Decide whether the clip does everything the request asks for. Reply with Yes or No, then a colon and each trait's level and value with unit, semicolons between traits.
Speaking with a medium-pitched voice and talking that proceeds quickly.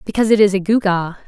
No: high, 200 Hz; fast, 235 wpm